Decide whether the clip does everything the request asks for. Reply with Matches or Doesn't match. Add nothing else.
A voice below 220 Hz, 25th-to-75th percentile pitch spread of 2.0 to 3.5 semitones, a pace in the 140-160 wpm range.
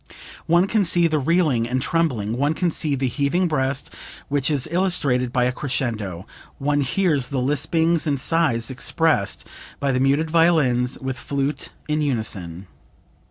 Doesn't match